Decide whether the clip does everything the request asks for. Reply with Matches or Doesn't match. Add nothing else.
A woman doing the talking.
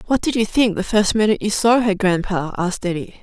Matches